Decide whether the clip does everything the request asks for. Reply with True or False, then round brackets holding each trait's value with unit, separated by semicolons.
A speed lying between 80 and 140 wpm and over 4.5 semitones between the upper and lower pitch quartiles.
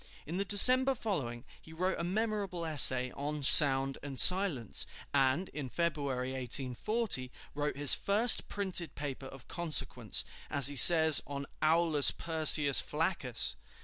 True (135 wpm; 5.1 semitones)